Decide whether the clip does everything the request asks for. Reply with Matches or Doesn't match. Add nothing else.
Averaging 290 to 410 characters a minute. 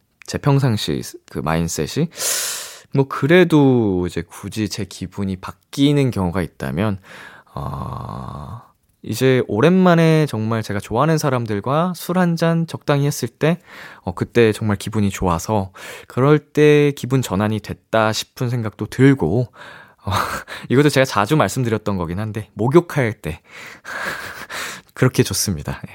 Doesn't match